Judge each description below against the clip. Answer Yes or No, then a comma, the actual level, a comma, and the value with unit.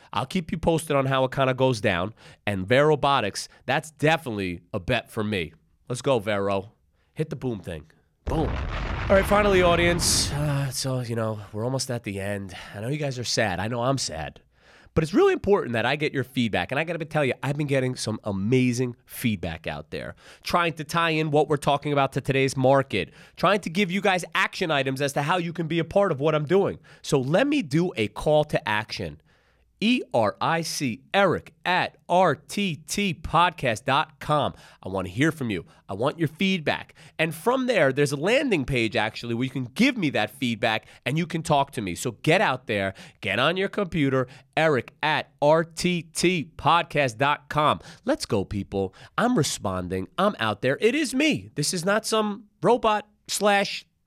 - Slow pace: No, average, 195 wpm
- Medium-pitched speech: Yes, medium, 145 Hz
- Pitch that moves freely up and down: Yes, wide, 6.4 semitones